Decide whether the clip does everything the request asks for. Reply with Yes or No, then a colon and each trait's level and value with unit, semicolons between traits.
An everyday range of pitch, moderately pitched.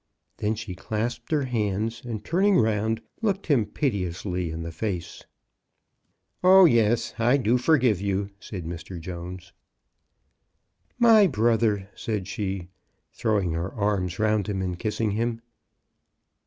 No: average, 4.0 semitones; low, 105 Hz